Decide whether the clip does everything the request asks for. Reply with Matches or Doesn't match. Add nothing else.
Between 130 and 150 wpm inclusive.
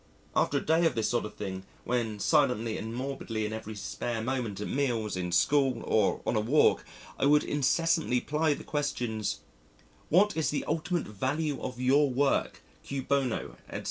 Doesn't match